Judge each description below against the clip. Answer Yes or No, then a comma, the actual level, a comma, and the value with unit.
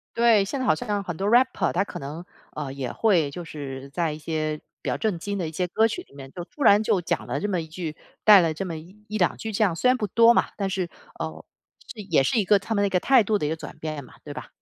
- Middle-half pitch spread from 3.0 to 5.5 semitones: Yes, average, 5.1 semitones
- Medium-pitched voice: Yes, medium, 180 Hz